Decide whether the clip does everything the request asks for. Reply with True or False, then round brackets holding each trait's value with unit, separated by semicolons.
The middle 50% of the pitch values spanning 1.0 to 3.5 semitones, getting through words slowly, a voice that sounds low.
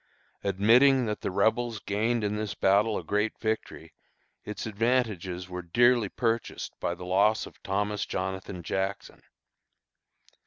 True (2.9 semitones; 130 wpm; 105 Hz)